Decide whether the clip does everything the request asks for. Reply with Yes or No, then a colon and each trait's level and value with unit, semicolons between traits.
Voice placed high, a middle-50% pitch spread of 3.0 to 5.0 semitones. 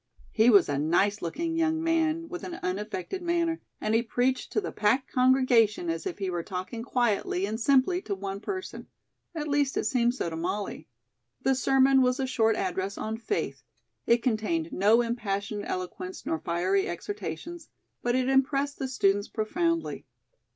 No: high, 230 Hz; wide, 5.5 semitones